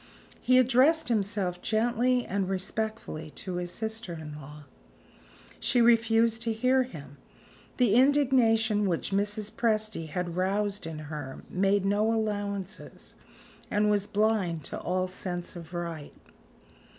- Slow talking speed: Yes, slow, 125 wpm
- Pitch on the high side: Yes, high, 205 Hz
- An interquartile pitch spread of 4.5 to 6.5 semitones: No, average, 4.1 semitones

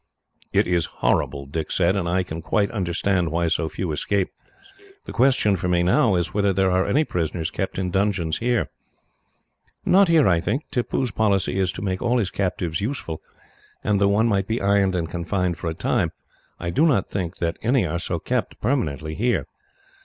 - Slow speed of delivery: No, average, 190 wpm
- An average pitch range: Yes, average, 3.6 semitones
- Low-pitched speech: Yes, very low, 95 Hz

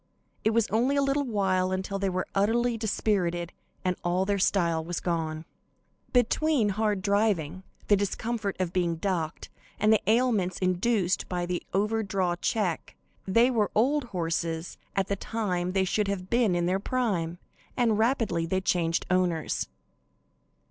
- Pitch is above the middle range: Yes, high, 195 Hz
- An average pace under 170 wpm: Yes, average, 155 wpm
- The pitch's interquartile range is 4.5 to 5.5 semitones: No, average, 3.8 semitones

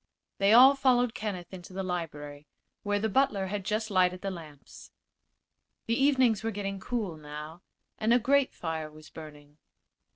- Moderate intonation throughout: No, wide, 5.9 semitones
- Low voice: No, high, 195 Hz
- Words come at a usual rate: Yes, average, 160 wpm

